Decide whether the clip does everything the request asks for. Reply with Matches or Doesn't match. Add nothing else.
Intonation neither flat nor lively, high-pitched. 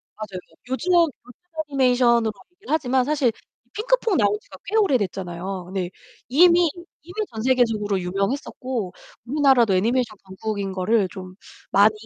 Doesn't match